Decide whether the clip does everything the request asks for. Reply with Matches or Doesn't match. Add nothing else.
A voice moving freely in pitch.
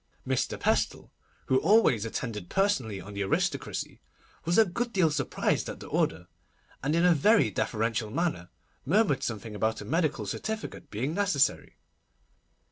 Matches